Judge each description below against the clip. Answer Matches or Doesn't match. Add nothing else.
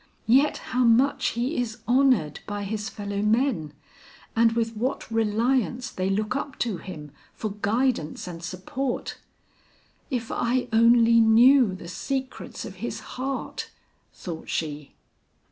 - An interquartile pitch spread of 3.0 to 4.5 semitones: Matches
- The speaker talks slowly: Matches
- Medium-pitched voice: Doesn't match